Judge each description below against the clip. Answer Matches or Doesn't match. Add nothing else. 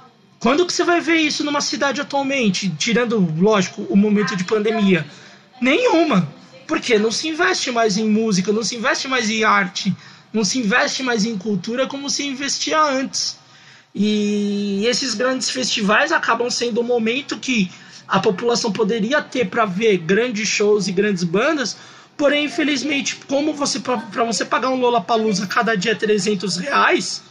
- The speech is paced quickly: Doesn't match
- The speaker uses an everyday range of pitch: Matches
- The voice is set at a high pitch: Matches